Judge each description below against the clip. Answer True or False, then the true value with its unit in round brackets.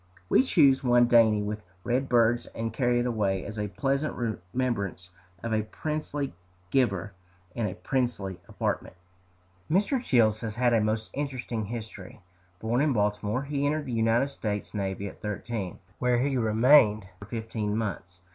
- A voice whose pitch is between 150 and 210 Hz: False (115 Hz)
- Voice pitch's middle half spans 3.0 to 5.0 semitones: True (3.6 semitones)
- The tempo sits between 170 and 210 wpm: False (155 wpm)